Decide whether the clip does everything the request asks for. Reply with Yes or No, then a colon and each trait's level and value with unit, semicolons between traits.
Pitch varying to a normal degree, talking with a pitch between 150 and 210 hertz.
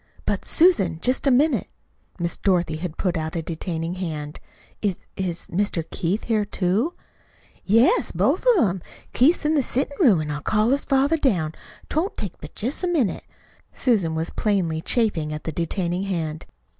No: wide, 7.2 semitones; high, 190 Hz